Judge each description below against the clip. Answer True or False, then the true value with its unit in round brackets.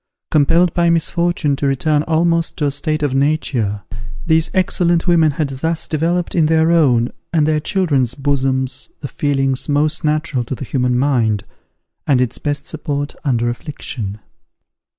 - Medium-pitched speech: True (145 Hz)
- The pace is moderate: True (150 wpm)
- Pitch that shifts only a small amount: False (3.4 semitones)